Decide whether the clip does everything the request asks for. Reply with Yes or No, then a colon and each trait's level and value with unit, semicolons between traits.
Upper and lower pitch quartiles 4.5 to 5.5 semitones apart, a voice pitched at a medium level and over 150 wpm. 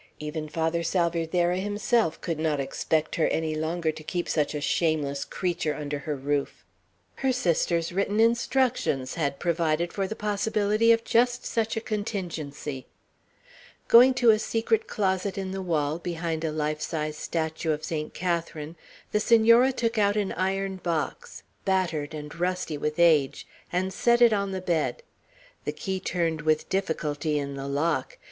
Yes: average, 4.8 semitones; medium, 170 Hz; average, 160 wpm